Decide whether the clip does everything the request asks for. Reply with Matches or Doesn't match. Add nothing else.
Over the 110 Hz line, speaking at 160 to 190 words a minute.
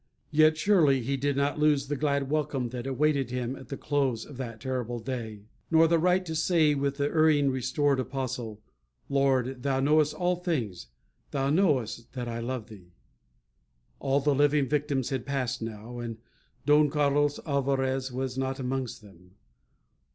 Matches